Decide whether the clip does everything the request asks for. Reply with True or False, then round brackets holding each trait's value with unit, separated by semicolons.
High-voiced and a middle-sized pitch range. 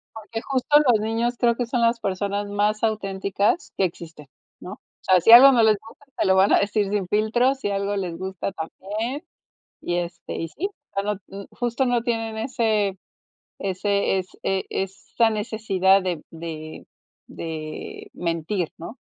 True (205 Hz; 3.2 semitones)